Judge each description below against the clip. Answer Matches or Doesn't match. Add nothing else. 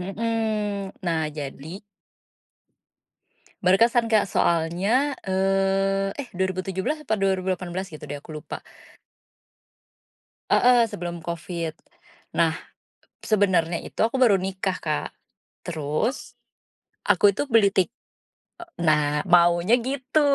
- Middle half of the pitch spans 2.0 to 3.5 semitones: Doesn't match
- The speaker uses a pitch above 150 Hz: Matches